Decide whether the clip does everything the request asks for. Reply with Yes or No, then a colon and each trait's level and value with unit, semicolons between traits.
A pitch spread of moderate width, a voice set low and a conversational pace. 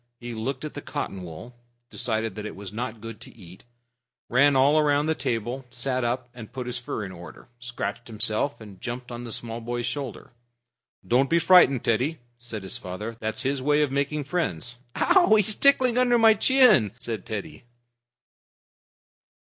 Yes: average, 4.6 semitones; low, 120 Hz; average, 175 wpm